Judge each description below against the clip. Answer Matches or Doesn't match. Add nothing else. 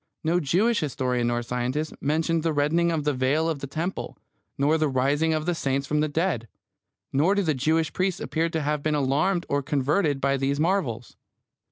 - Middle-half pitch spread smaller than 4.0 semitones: Matches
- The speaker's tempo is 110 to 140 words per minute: Doesn't match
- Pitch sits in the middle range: Matches